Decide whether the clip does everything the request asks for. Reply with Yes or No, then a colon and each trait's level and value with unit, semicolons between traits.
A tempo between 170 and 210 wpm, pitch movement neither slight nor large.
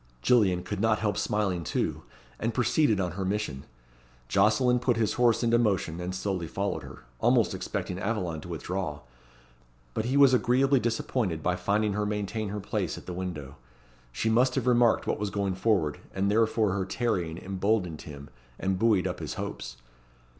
Yes: average, 175 wpm; average, 4.0 semitones